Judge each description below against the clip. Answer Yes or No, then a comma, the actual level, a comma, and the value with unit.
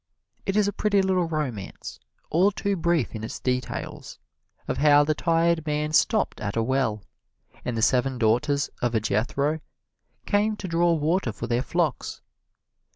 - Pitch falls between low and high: Yes, medium, 150 Hz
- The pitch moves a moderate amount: No, wide, 6.0 semitones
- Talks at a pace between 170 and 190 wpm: No, average, 155 wpm